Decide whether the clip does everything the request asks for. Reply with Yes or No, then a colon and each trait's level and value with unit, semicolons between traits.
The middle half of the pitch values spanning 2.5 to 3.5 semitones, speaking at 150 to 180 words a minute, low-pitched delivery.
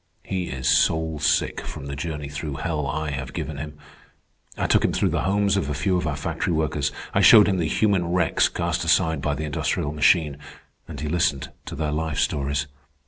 No: average, 2.8 semitones; fast, 205 wpm; very low, 75 Hz